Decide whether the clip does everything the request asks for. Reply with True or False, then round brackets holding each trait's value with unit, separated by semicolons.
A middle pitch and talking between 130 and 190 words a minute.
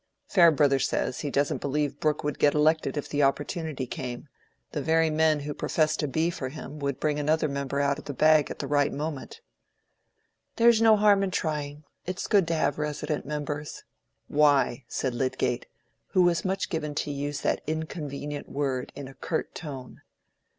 True (150 Hz; 180 wpm)